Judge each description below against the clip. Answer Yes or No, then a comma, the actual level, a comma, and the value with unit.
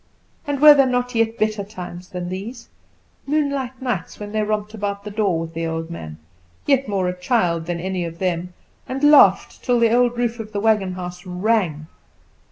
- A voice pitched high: Yes, high, 205 Hz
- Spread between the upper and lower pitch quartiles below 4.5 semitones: No, average, 5.1 semitones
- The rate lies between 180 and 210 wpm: Yes, average, 190 wpm